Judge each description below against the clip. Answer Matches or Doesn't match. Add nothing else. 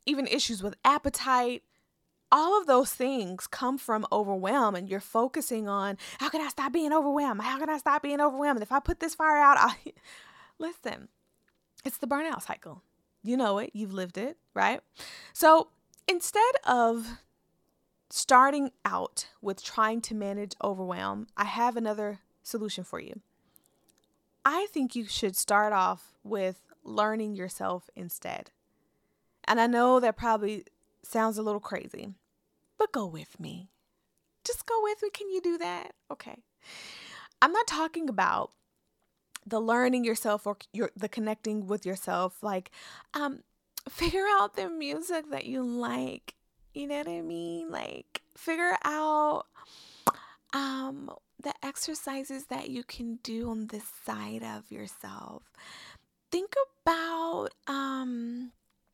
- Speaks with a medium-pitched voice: Doesn't match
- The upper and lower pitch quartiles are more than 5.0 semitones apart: Matches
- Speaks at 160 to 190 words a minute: Doesn't match